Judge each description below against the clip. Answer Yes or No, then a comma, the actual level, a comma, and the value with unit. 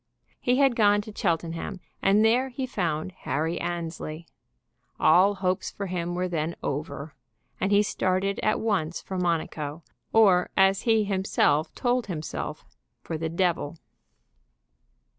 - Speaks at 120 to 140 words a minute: Yes, slow, 135 wpm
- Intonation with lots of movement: No, average, 3.8 semitones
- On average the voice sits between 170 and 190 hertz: Yes, medium, 185 Hz